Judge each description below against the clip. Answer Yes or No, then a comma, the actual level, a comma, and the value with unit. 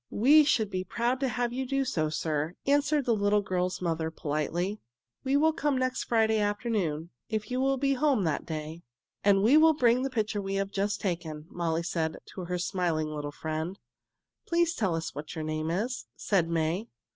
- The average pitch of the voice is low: No, high, 195 Hz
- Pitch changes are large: Yes, wide, 7.5 semitones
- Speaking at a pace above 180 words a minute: Yes, average, 195 wpm